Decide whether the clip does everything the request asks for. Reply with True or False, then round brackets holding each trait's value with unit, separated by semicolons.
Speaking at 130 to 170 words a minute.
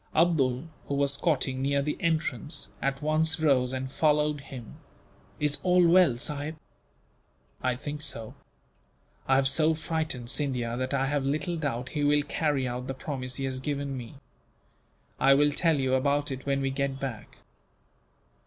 True (165 wpm)